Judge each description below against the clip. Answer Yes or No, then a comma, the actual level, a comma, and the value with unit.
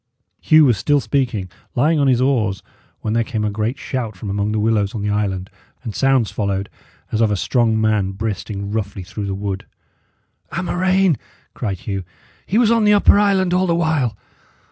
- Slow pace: No, average, 190 wpm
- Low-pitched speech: Yes, low, 110 Hz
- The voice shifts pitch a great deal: Yes, wide, 6.0 semitones